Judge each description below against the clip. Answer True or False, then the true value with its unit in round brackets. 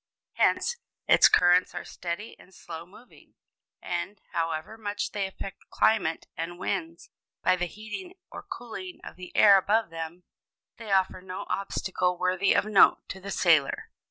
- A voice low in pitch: False (185 Hz)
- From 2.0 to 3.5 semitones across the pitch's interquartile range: True (2.9 semitones)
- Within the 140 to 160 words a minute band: True (155 wpm)